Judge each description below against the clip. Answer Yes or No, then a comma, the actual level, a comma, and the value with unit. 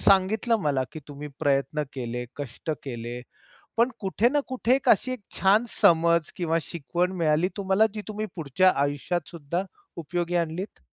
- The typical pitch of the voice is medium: Yes, medium, 170 Hz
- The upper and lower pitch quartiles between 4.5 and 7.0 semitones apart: Yes, wide, 5.5 semitones